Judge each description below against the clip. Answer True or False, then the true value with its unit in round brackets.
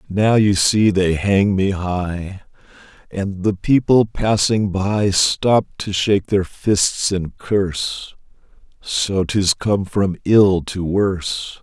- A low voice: True (95 Hz)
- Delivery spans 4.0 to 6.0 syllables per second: False (3.1 syllables/s)